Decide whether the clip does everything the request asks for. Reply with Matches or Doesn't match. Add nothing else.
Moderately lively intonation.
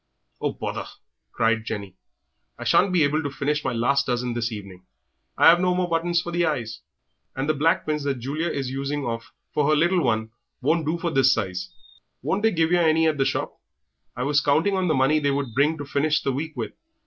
Matches